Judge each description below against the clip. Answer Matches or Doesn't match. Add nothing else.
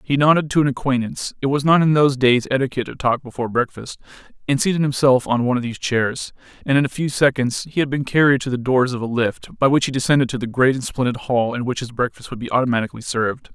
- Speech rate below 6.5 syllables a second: Doesn't match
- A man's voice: Matches